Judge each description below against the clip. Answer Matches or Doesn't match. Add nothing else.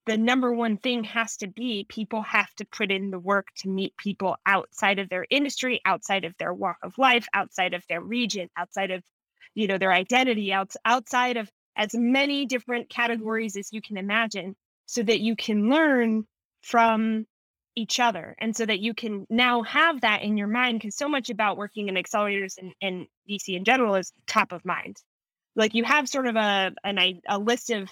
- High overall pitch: Matches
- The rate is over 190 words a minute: Matches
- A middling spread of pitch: Matches